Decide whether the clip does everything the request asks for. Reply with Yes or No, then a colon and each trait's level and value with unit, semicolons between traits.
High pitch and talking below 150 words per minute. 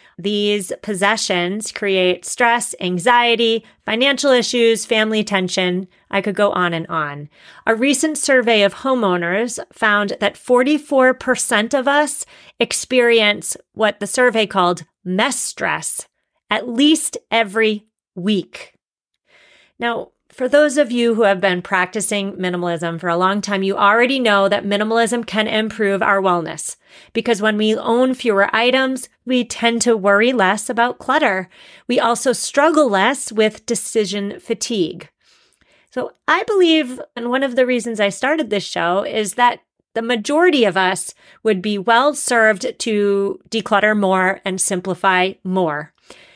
Yes: high, 220 Hz; average, 140 wpm